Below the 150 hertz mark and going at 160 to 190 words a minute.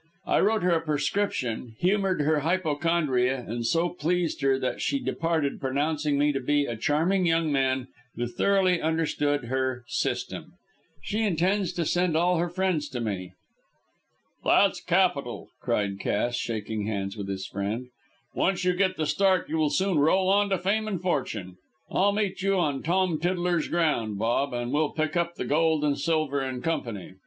No: medium, 155 Hz; average, 170 wpm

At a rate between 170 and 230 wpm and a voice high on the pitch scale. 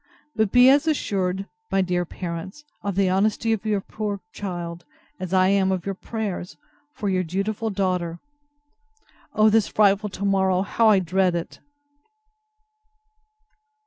No: average, 145 wpm; high, 195 Hz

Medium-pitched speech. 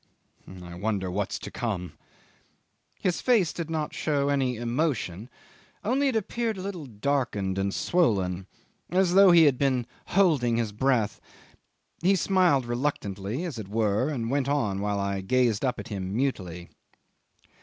No: low, 125 Hz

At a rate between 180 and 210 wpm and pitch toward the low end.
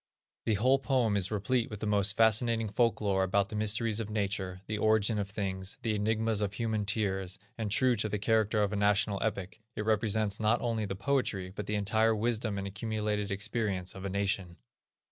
Yes: average, 200 wpm; low, 105 Hz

